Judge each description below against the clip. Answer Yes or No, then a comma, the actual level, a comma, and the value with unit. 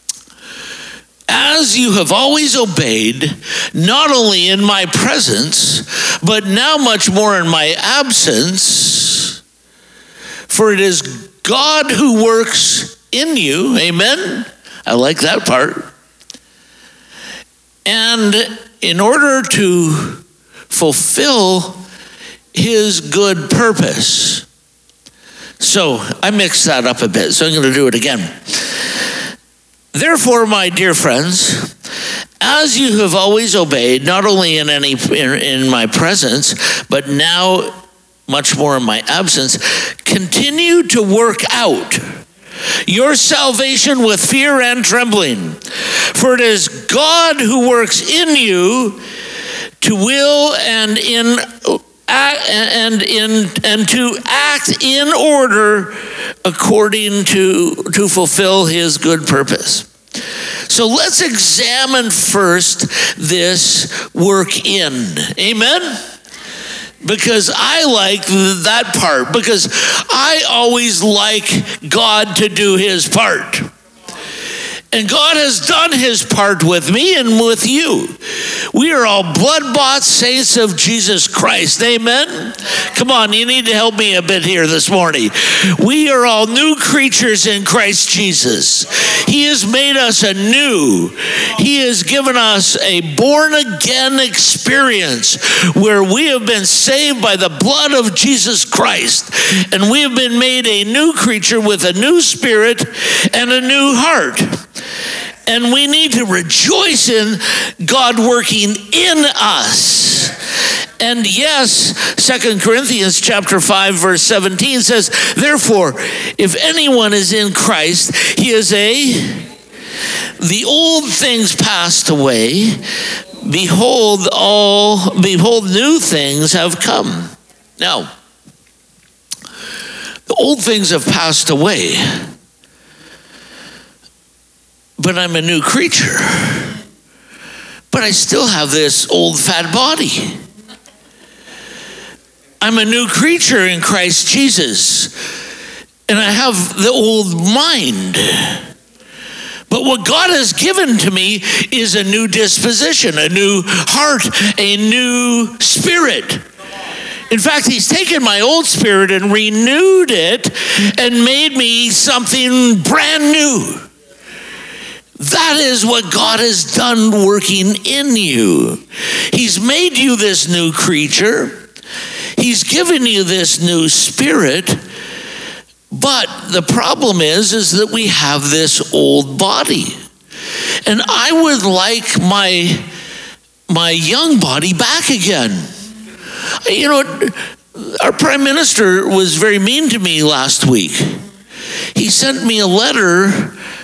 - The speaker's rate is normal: No, slow, 120 wpm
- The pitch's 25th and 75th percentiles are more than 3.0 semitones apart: Yes, average, 5.1 semitones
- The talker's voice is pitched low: No, high, 215 Hz